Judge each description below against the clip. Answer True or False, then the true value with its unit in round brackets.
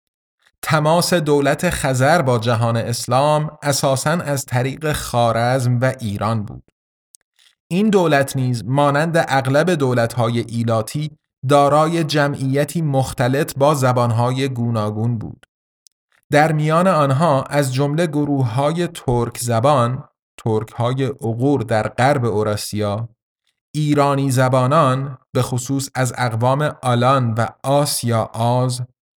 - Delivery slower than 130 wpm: True (105 wpm)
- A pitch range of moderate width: True (3.5 semitones)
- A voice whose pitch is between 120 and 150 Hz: True (135 Hz)